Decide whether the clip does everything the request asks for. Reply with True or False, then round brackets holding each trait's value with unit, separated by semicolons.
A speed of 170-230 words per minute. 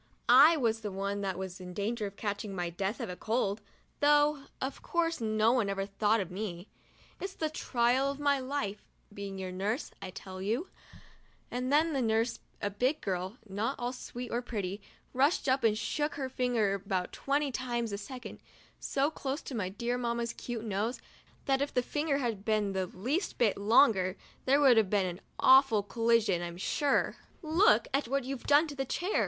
True (195 wpm)